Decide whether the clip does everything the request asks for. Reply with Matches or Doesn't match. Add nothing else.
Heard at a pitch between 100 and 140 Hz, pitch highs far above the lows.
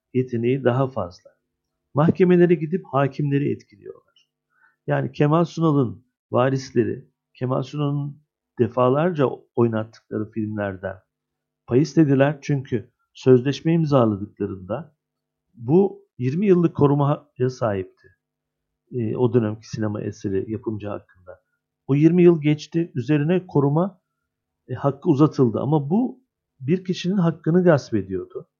Matches